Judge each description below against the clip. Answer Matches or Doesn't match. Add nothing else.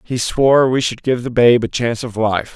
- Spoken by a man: Matches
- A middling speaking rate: Doesn't match